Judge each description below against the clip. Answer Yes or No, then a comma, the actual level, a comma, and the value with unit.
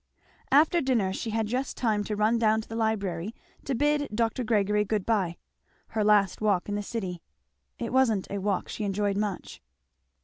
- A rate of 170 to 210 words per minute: Yes, average, 180 wpm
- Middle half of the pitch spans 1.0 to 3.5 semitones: Yes, narrow, 2.4 semitones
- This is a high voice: Yes, high, 215 Hz